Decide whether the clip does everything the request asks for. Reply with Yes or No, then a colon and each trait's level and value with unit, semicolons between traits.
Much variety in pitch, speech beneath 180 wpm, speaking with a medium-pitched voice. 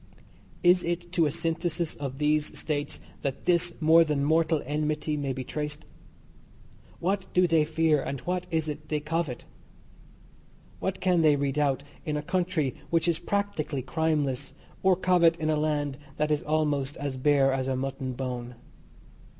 No: average, 2.8 semitones; average, 160 wpm; medium, 155 Hz